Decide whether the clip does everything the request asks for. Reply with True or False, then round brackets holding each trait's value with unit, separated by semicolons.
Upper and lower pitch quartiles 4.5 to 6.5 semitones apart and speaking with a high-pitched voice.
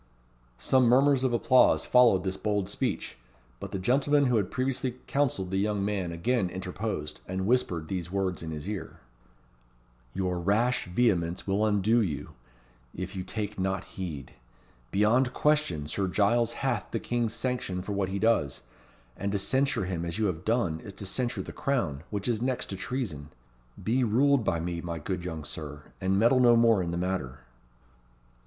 False (5.0 semitones; 100 Hz)